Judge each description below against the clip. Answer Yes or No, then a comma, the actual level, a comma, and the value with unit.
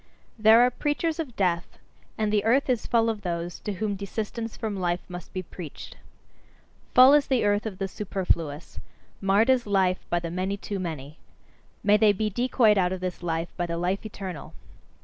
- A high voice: Yes, high, 200 Hz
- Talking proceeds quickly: No, average, 190 wpm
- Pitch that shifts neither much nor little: Yes, average, 3.8 semitones